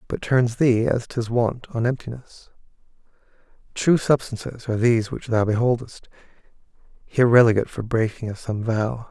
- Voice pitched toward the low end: Yes, low, 120 Hz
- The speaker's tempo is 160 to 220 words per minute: No, average, 145 wpm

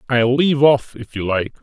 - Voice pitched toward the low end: Yes, low, 125 Hz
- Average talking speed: No, fast, 220 wpm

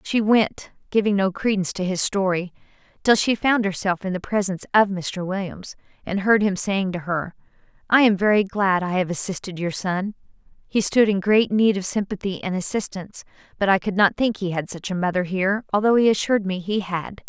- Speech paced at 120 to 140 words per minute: No, fast, 205 wpm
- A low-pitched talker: No, high, 195 Hz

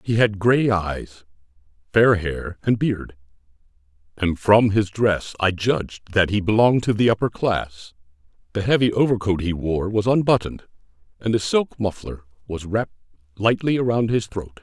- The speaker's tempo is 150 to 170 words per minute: Yes, average, 155 wpm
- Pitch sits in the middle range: No, low, 100 Hz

